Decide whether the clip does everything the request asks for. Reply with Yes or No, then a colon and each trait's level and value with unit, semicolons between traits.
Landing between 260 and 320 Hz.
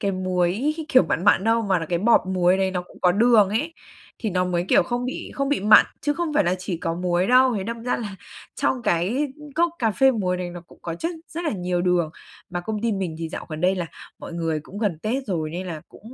No: high, 190 Hz